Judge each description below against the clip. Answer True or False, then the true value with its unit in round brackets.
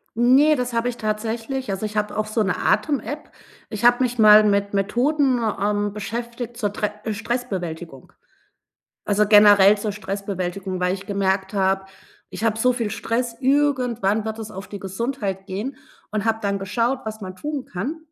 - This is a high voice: True (215 Hz)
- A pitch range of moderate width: True (3.4 semitones)